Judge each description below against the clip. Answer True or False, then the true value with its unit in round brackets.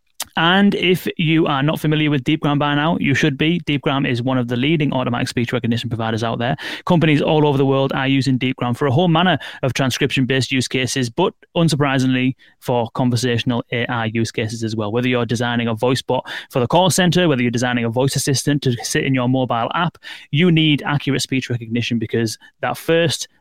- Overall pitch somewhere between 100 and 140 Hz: True (135 Hz)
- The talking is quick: True (210 wpm)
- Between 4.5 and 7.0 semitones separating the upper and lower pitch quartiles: False (4.1 semitones)